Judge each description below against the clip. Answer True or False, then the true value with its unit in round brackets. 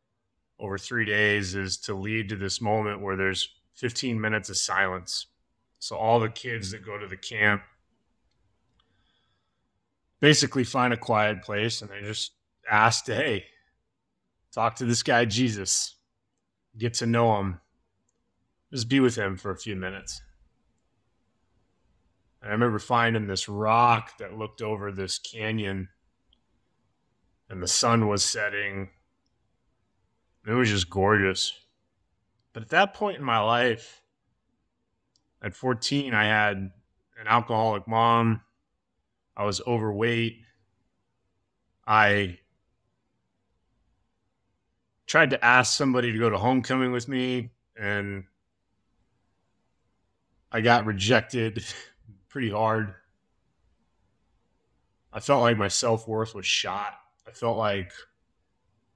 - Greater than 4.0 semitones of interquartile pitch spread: False (3.2 semitones)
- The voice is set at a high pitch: False (110 Hz)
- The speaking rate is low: True (120 wpm)